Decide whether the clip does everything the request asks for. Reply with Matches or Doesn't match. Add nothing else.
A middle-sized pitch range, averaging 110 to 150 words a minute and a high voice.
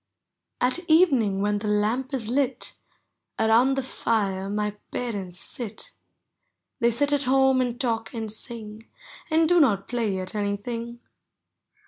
Matches